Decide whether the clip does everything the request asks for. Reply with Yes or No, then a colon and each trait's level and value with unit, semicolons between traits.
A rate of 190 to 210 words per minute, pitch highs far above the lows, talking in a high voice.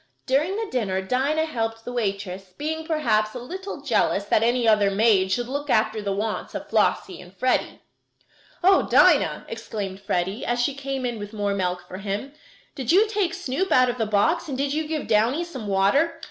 Yes: average, 195 wpm; wide, 5.9 semitones; high, 240 Hz